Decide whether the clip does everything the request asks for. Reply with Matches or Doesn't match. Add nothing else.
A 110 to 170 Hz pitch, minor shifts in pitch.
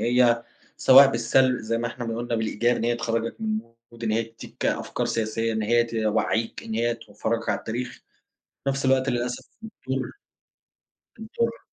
Matches